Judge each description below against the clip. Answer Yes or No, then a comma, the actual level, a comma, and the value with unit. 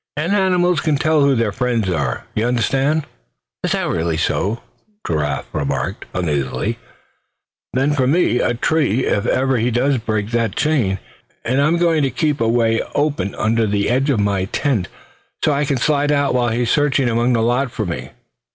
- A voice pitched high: No, low, 120 Hz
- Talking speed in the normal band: Yes, average, 180 wpm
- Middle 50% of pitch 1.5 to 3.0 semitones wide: No, wide, 5.5 semitones